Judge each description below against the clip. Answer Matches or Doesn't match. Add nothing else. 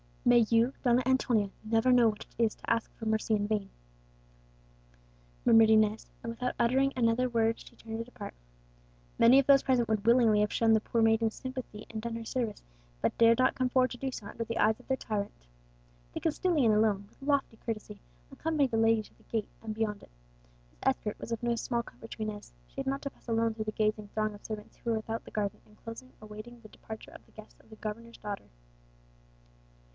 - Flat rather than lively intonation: Matches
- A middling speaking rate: Doesn't match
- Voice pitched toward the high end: Matches